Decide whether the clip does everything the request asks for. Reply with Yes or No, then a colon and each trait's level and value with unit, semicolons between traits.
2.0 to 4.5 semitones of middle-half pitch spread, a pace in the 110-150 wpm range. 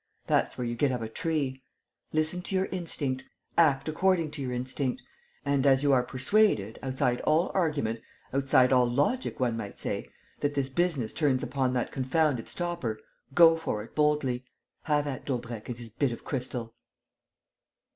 No: average, 3.8 semitones; average, 165 wpm